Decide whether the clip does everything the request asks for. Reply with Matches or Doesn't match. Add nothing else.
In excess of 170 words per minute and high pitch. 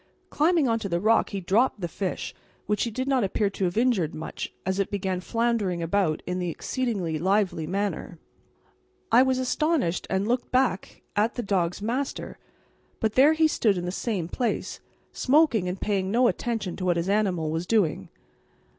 Matches